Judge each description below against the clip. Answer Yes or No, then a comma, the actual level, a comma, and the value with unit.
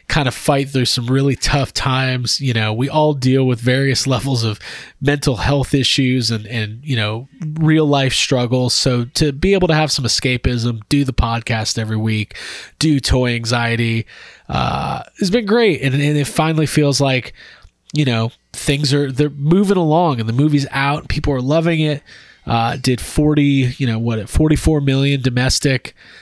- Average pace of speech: Yes, average, 180 wpm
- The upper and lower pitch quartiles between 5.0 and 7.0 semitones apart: No, average, 3.3 semitones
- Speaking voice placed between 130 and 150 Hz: Yes, low, 135 Hz